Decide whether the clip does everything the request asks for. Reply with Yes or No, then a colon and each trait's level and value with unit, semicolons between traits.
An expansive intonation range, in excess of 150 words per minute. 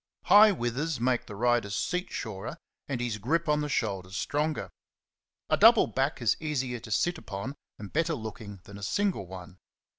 Yes: wide, 6.8 semitones; average, 180 wpm